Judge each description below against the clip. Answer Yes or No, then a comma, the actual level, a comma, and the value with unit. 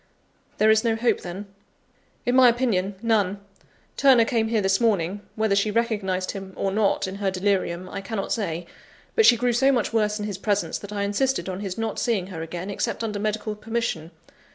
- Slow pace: No, average, 200 wpm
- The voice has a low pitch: No, high, 210 Hz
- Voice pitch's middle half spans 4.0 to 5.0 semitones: No, average, 2.8 semitones